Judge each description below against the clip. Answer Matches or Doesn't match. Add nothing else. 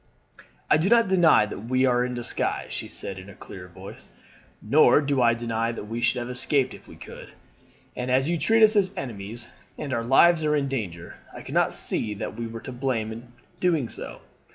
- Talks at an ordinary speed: Doesn't match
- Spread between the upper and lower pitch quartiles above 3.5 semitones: Matches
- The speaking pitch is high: Doesn't match